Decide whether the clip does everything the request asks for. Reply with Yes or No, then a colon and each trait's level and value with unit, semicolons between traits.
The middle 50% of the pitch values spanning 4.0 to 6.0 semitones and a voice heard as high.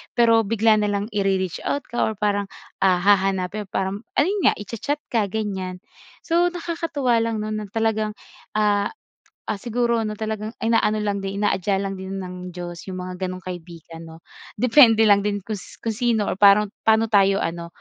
No: average, 2.8 semitones; high, 205 Hz